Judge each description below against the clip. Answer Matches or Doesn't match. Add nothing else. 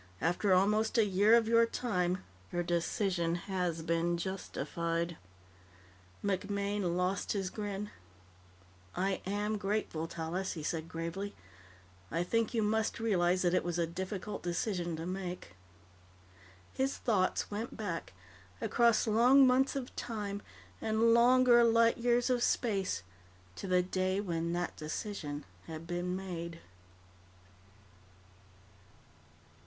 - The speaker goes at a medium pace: Doesn't match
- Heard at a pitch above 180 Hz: Matches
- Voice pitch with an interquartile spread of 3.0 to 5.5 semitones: Matches